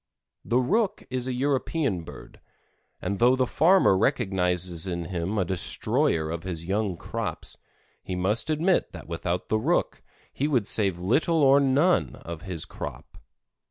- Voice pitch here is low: Yes, low, 105 Hz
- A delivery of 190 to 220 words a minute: No, average, 155 wpm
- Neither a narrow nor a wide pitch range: No, wide, 7.3 semitones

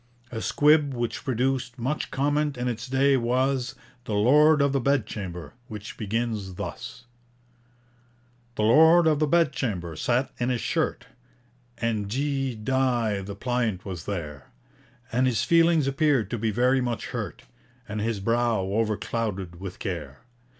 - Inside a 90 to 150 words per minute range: Yes, average, 145 wpm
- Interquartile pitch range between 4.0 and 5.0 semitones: Yes, average, 4.3 semitones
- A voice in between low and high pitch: No, low, 120 Hz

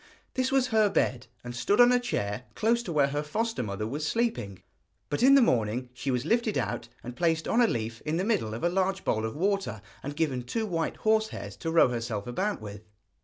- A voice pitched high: No, medium, 155 Hz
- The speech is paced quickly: Yes, fast, 225 wpm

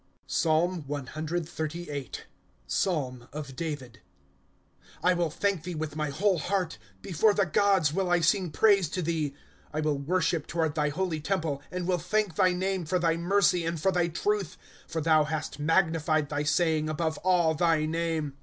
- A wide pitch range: No, average, 3.0 semitones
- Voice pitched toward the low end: No, medium, 165 Hz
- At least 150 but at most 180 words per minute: Yes, average, 175 wpm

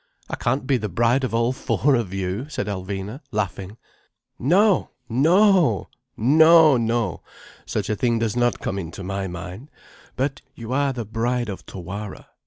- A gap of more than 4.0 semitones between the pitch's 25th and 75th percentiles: Yes, average, 5.1 semitones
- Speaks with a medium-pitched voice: No, low, 115 Hz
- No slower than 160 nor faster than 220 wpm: No, average, 150 wpm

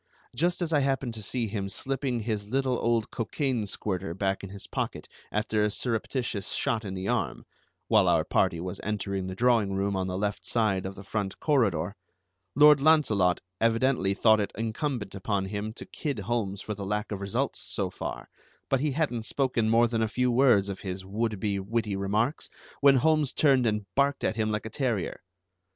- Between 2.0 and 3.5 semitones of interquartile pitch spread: No, average, 4.2 semitones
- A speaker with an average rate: Yes, average, 195 wpm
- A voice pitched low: Yes, low, 110 Hz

